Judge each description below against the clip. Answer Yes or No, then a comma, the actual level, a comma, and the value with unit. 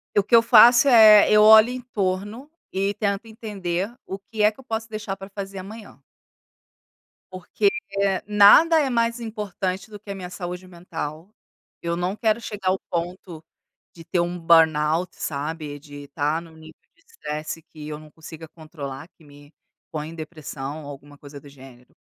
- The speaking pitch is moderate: Yes, medium, 180 Hz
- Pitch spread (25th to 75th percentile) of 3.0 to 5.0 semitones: No, wide, 5.4 semitones